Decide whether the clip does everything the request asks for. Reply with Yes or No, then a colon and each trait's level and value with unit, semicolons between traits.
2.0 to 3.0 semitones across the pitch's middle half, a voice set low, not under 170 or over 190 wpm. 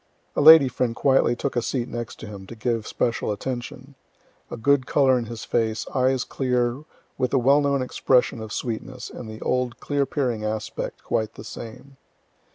Yes: average, 2.7 semitones; low, 125 Hz; average, 175 wpm